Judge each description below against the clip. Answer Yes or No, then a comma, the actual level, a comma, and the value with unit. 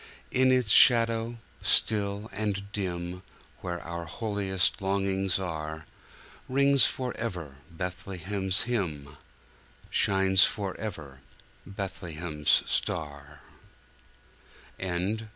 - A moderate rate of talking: No, slow, 70 wpm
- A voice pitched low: Yes, very low, 95 Hz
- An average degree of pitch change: Yes, average, 3.7 semitones